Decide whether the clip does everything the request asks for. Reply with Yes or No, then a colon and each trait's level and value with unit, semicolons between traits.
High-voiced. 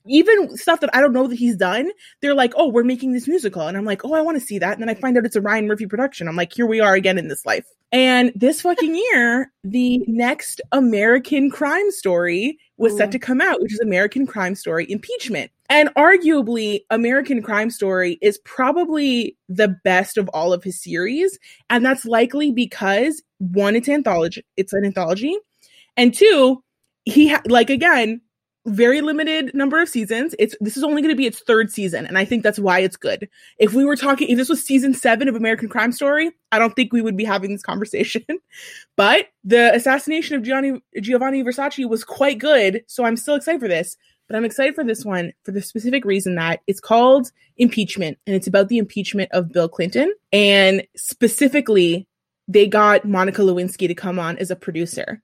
Yes: high, 235 Hz